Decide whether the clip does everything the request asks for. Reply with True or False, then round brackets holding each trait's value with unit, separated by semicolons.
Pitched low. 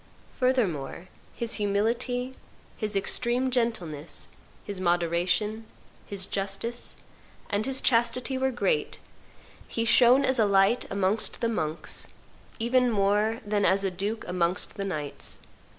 False (210 Hz)